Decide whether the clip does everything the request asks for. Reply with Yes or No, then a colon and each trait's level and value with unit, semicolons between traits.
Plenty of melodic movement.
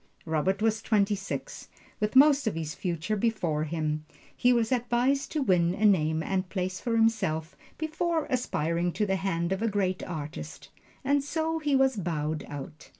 Yes: wide, 6.5 semitones